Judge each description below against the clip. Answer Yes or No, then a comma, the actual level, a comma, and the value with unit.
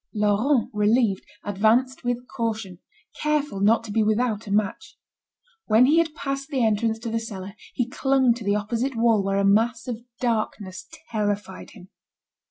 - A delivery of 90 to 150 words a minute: No, average, 165 wpm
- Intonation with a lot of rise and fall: No, average, 3.3 semitones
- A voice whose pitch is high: Yes, high, 225 Hz